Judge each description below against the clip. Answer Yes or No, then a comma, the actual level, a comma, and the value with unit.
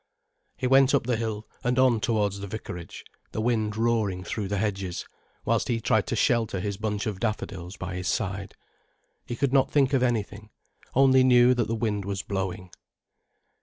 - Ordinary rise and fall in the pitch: Yes, average, 3.6 semitones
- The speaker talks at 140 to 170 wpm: No, average, 180 wpm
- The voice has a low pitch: Yes, low, 110 Hz